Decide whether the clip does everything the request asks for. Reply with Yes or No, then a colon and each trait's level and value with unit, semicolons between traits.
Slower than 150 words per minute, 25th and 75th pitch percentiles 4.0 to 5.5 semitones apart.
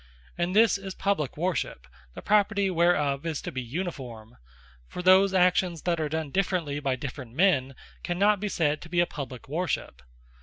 No: average, 175 wpm; average, 5.0 semitones